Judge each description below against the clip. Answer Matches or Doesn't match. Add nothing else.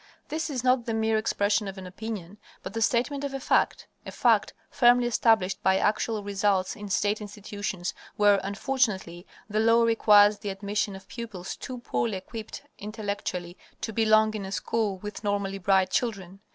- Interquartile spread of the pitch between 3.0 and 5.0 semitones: Doesn't match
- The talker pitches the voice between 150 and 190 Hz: Doesn't match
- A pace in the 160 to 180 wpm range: Matches